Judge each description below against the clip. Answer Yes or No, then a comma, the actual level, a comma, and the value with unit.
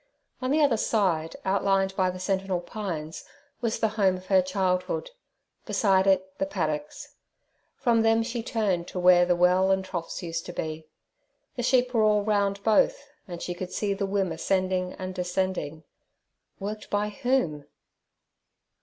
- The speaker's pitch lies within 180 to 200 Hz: Yes, high, 190 Hz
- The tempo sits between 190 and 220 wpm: No, average, 155 wpm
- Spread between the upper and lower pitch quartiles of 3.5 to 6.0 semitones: No, average, 2.8 semitones